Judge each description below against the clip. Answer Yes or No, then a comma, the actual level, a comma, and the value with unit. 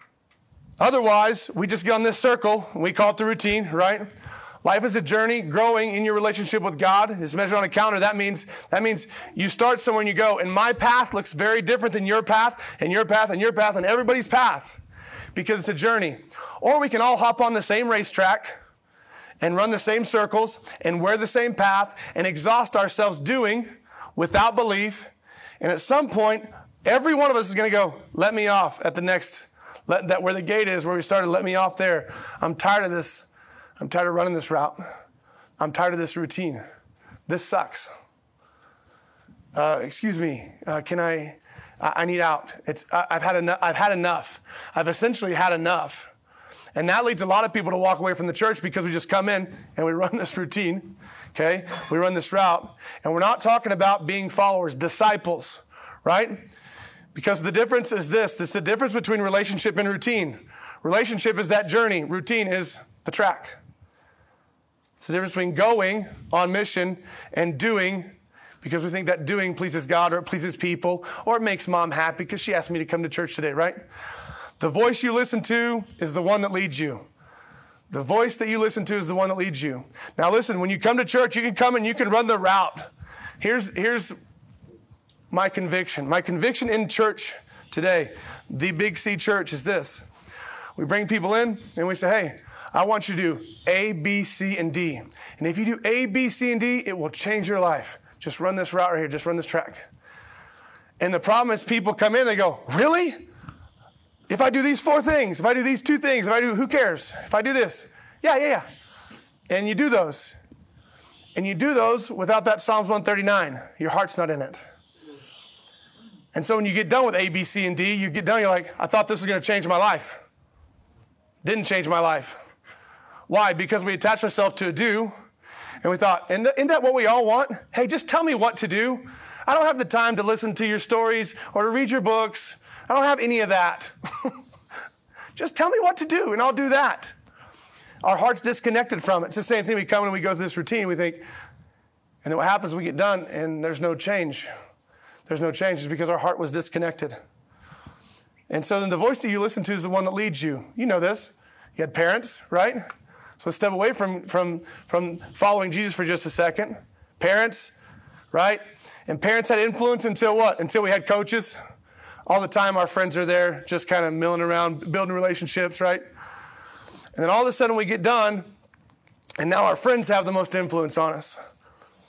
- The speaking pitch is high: Yes, high, 200 Hz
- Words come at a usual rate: No, fast, 210 wpm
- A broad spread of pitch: No, average, 4.3 semitones